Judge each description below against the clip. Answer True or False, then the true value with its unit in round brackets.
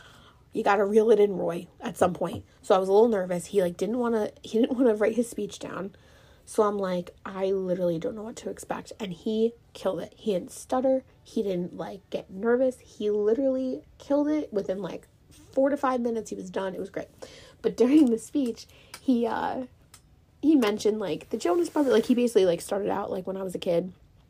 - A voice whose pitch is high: True (220 Hz)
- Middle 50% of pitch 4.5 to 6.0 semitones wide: True (4.8 semitones)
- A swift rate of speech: True (225 wpm)